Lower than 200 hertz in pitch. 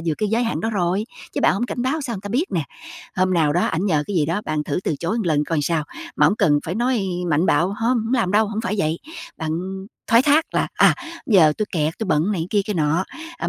Yes: high, 190 Hz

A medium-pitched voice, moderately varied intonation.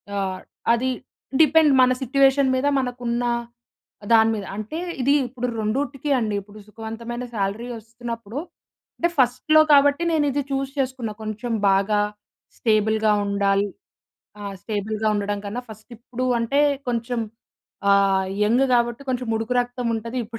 No: high, 235 Hz; average, 3.2 semitones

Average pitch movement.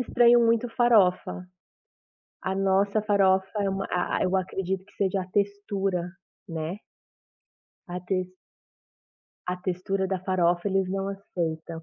No: narrow, 1.7 semitones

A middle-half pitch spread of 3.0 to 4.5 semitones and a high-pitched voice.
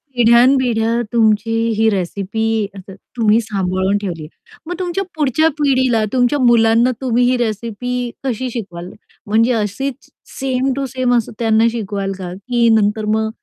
Yes: average, 3.4 semitones; high, 225 Hz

